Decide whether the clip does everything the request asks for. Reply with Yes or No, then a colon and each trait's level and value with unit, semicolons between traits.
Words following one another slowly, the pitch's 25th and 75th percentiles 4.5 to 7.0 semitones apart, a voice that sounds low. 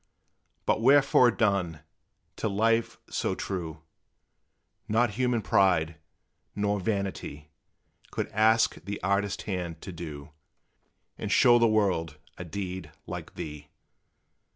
Yes: slow, 110 wpm; average, 4.9 semitones; low, 100 Hz